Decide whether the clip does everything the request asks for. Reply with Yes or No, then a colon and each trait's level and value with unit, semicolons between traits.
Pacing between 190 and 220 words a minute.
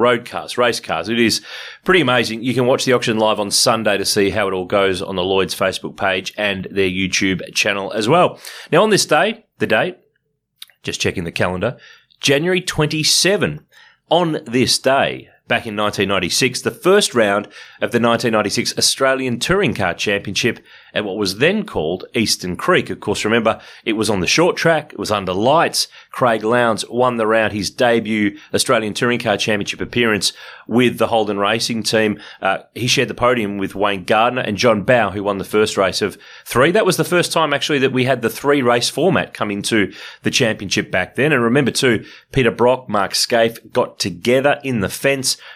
Yes: average, 195 wpm